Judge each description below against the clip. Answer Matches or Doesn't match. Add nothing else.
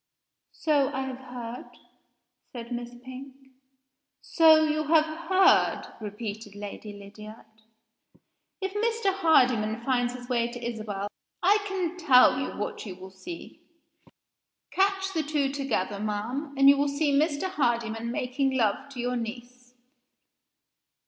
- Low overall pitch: Doesn't match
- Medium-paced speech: Doesn't match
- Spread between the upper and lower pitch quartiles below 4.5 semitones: Doesn't match